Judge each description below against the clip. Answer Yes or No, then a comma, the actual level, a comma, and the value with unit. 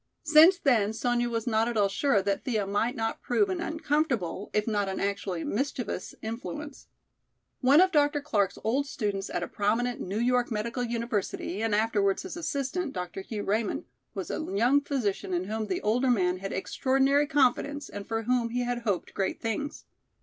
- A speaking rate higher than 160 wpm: Yes, average, 180 wpm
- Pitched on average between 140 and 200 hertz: No, high, 230 Hz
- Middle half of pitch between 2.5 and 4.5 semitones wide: No, average, 5.0 semitones